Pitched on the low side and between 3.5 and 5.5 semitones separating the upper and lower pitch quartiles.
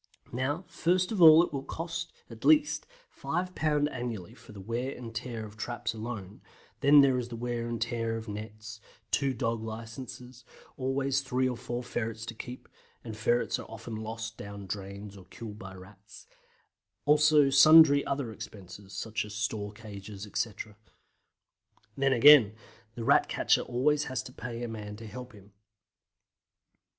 Yes: low, 115 Hz; average, 3.9 semitones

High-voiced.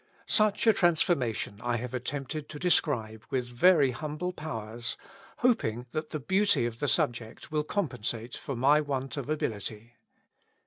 No: low, 135 Hz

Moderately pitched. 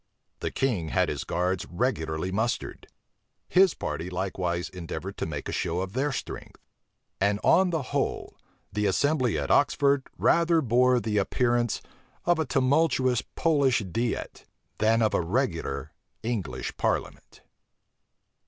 No: low, 115 Hz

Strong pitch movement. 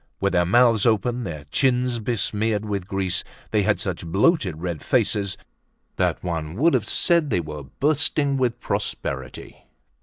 Yes: wide, 5.8 semitones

